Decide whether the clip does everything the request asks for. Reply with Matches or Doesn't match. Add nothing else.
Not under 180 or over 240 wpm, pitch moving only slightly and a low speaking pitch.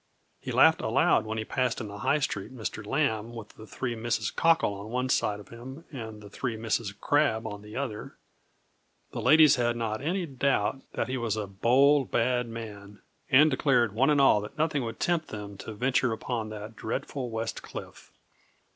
Doesn't match